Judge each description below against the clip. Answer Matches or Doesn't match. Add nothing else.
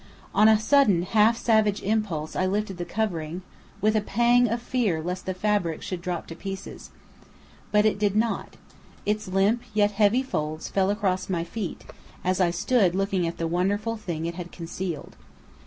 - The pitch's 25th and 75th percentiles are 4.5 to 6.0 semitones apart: Doesn't match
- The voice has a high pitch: Matches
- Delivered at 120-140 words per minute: Doesn't match